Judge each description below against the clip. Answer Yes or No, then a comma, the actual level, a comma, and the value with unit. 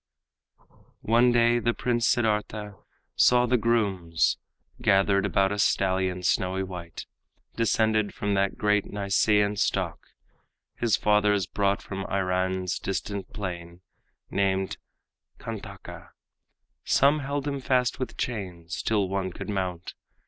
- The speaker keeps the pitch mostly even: No, average, 3.3 semitones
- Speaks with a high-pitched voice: No, low, 100 Hz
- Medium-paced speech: No, slow, 115 wpm